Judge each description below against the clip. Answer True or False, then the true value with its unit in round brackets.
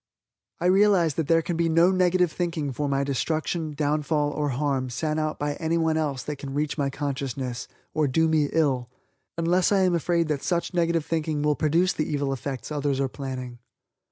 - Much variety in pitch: False (3.1 semitones)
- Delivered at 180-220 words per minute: True (190 wpm)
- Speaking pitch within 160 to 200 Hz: False (150 Hz)